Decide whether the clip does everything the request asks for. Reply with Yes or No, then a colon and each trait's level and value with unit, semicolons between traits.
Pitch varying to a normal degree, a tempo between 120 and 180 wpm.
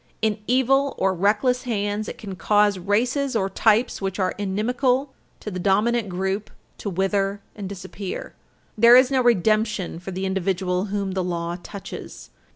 Yes: average, 3.5 semitones; average, 160 wpm